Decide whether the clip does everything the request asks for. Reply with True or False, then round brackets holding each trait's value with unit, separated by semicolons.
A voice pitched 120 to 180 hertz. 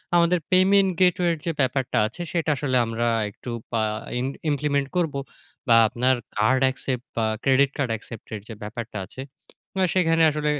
True (135 Hz)